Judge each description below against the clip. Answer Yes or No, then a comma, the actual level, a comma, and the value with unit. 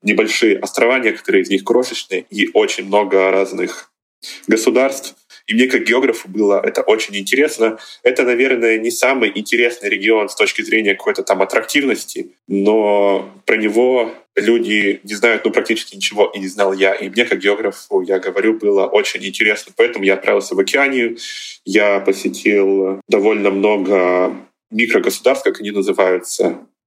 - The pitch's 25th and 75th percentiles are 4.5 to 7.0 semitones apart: Yes, wide, 5.4 semitones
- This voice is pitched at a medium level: No, low, 110 Hz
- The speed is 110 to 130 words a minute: No, average, 145 wpm